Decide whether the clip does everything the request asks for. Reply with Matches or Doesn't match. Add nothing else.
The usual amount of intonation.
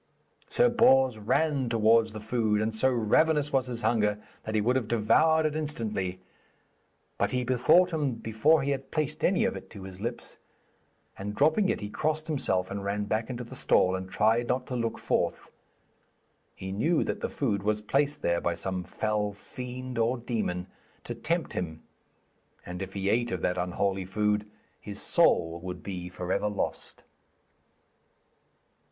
Matches